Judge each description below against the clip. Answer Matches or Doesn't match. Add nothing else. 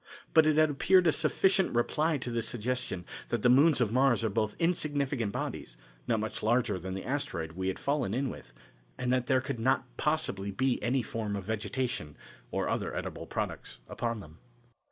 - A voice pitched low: Matches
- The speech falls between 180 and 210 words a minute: Matches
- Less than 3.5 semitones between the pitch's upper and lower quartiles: Doesn't match